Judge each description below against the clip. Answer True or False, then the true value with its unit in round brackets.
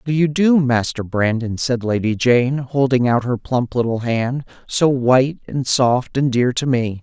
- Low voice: True (125 Hz)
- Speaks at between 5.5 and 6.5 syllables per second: False (4.5 syllables/s)